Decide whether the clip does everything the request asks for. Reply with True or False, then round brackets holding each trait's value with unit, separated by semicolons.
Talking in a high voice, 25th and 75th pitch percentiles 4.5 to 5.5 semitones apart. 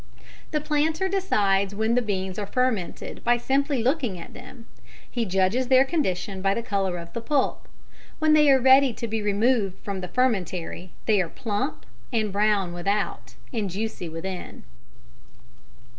True (215 Hz; 5.2 semitones)